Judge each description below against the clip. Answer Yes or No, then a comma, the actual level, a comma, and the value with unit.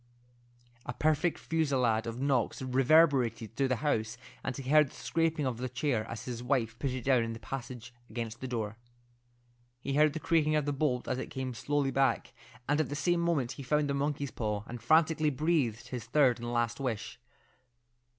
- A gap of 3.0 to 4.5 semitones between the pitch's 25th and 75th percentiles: Yes, average, 3.9 semitones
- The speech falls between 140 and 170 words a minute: No, average, 195 wpm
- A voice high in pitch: No, low, 130 Hz